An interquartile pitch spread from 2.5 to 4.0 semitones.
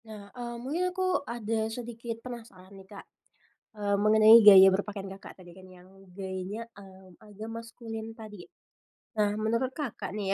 Yes: average, 2.9 semitones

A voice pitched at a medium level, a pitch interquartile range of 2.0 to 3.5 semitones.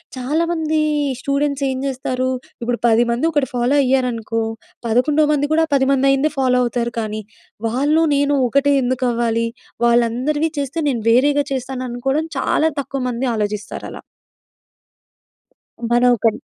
No: very high, 260 Hz; average, 3.2 semitones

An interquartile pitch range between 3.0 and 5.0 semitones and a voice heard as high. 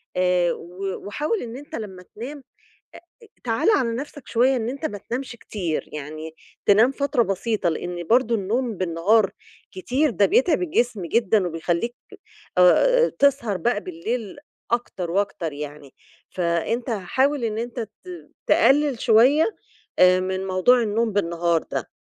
No: wide, 5.5 semitones; high, 220 Hz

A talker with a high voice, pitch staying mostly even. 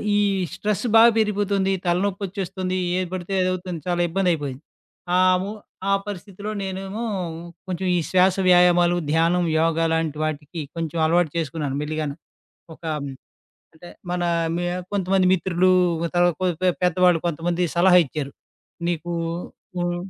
No: medium, 175 Hz; narrow, 2.2 semitones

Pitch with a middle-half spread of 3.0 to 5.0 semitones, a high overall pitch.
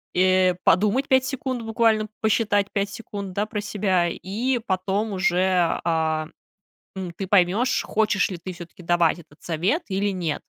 Yes: average, 3.3 semitones; high, 195 Hz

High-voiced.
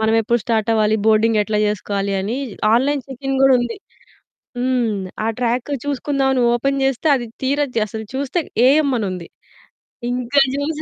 Yes: high, 245 Hz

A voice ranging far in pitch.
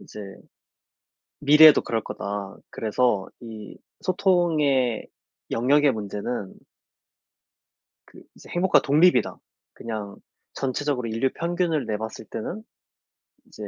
Yes: wide, 5.9 semitones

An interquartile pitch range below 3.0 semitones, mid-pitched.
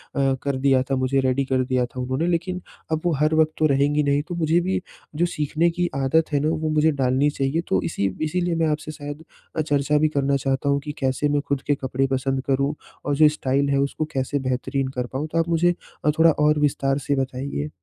Yes: narrow, 2.6 semitones; medium, 145 Hz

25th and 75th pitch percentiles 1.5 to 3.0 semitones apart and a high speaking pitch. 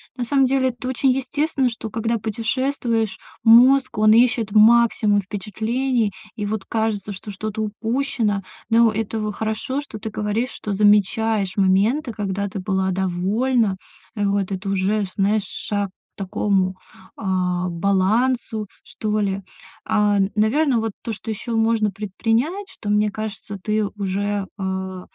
Yes: narrow, 2.6 semitones; high, 215 Hz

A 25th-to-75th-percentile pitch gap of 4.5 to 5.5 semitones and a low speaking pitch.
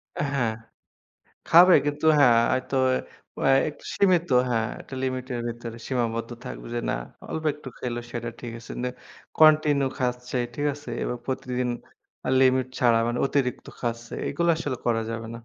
No: average, 3.3 semitones; low, 125 Hz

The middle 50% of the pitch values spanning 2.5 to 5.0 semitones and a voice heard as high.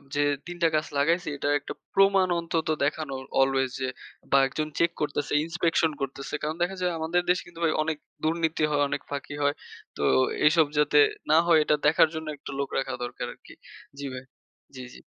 No: average, 2.8 semitones; medium, 155 Hz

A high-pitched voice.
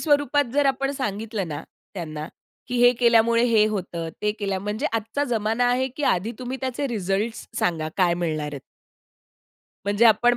Yes: high, 220 Hz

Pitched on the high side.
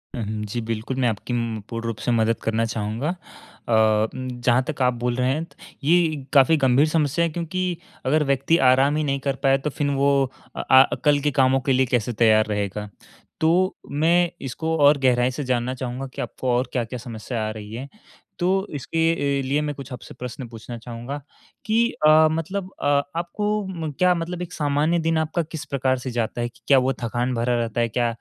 No: low, 130 Hz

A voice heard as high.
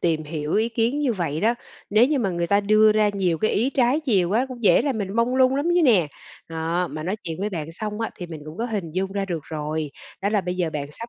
Yes: high, 200 Hz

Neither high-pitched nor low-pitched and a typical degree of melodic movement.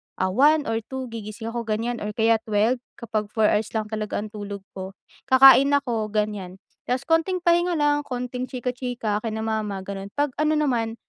No: high, 225 Hz; average, 3.7 semitones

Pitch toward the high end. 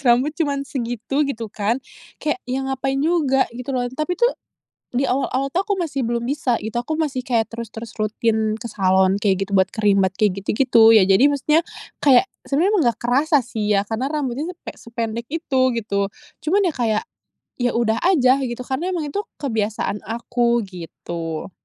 Yes: high, 245 Hz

